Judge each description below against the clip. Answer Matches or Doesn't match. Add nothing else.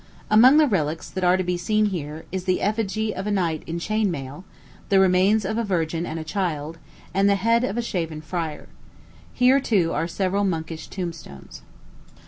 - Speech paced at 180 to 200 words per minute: Matches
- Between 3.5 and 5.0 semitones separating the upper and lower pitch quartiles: Matches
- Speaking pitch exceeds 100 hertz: Matches